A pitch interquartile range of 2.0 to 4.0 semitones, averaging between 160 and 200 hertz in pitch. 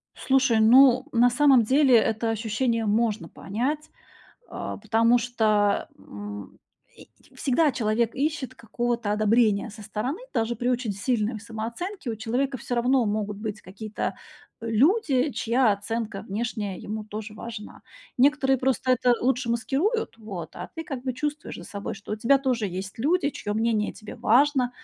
No: average, 3.5 semitones; high, 235 Hz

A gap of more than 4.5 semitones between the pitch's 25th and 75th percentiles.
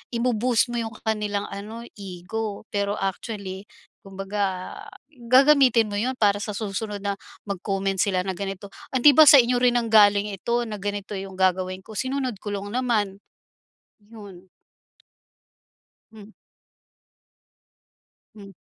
No: average, 2.8 semitones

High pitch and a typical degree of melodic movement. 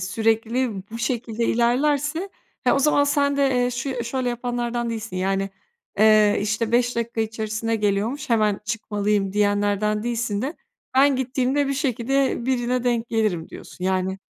Yes: high, 235 Hz; average, 3.4 semitones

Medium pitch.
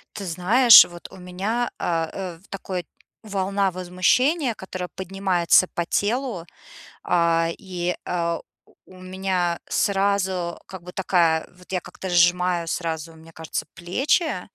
Yes: medium, 180 Hz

